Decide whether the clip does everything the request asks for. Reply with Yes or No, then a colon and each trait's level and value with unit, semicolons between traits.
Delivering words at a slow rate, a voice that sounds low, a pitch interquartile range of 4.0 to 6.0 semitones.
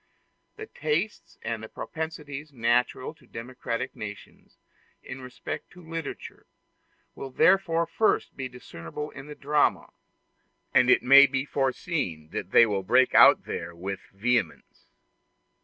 Yes: slow, 125 wpm; low, 130 Hz; average, 4.6 semitones